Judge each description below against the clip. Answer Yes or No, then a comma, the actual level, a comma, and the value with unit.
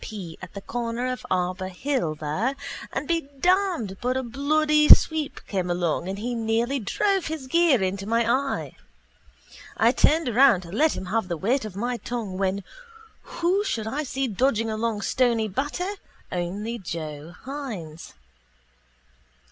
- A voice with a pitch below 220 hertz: No, high, 230 Hz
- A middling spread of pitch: No, wide, 6.5 semitones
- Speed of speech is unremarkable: Yes, average, 155 wpm